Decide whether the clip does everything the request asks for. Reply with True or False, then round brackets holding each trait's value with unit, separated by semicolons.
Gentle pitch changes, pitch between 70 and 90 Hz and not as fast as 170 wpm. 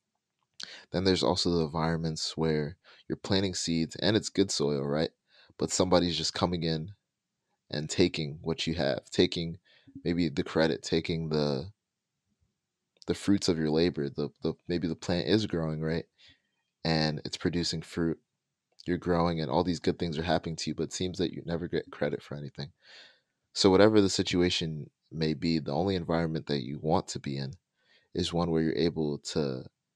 False (2.2 semitones; 80 Hz; 180 wpm)